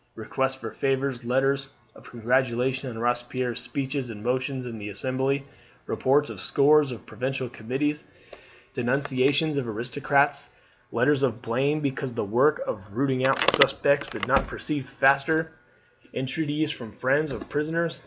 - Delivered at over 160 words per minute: No, average, 145 wpm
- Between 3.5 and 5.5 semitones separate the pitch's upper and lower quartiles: No, narrow, 2.6 semitones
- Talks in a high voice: No, low, 130 Hz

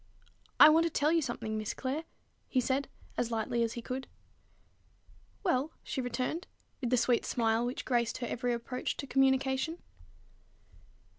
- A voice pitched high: Yes, very high, 255 Hz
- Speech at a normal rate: Yes, average, 155 wpm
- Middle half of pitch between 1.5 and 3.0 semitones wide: Yes, average, 2.7 semitones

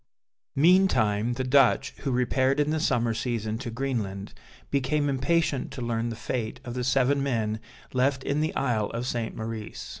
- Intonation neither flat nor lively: Yes, average, 3.3 semitones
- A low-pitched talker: Yes, low, 125 Hz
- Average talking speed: Yes, average, 170 wpm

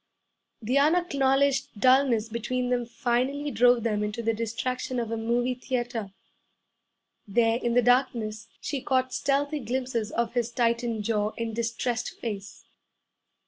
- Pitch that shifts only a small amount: Yes, narrow, 2.2 semitones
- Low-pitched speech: No, high, 240 Hz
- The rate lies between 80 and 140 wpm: Yes, slow, 135 wpm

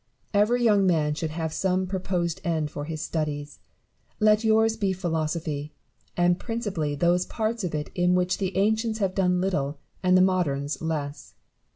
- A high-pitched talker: No, medium, 180 Hz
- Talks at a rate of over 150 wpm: Yes, average, 165 wpm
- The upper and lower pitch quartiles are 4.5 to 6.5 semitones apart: No, average, 4.0 semitones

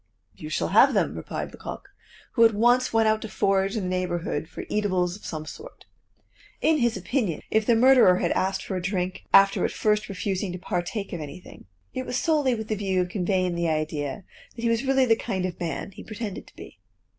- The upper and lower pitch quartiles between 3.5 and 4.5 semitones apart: Yes, average, 4.1 semitones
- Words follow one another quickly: Yes, fast, 215 wpm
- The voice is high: Yes, high, 195 Hz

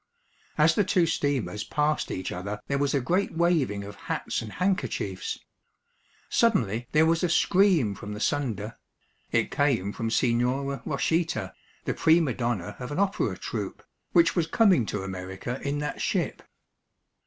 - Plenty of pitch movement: Yes, wide, 7.6 semitones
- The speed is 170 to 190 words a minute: No, average, 155 wpm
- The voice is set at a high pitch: No, medium, 140 Hz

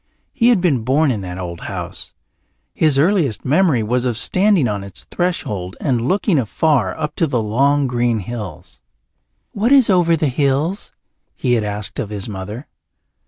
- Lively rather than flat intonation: Yes, wide, 7.2 semitones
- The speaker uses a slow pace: No, average, 165 wpm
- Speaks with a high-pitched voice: No, low, 130 Hz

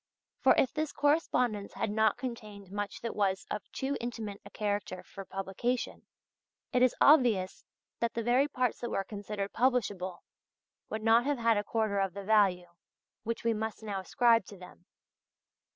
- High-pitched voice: Yes, high, 220 Hz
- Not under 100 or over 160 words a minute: No, average, 170 wpm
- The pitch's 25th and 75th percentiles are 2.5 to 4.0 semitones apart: Yes, average, 3.3 semitones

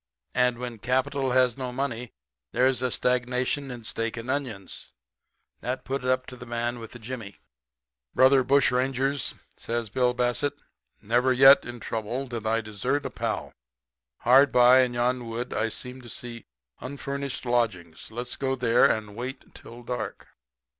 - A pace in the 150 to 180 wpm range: Yes, average, 160 wpm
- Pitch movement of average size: No, narrow, 1.8 semitones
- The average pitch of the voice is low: Yes, low, 125 Hz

